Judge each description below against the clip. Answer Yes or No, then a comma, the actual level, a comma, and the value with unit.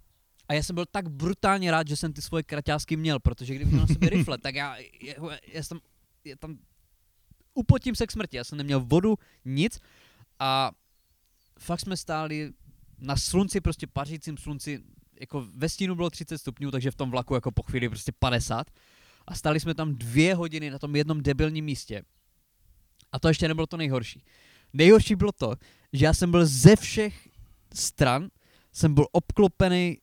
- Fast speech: Yes, fast, 180 wpm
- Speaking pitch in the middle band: Yes, medium, 150 Hz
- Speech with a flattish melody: No, average, 4.0 semitones